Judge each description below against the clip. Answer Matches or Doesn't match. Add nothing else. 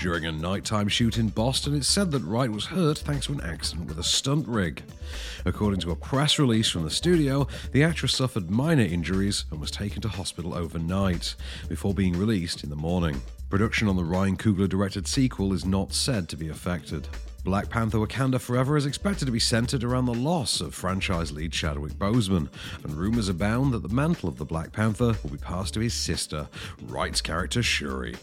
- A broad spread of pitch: Matches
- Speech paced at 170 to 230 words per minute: Matches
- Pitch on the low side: Matches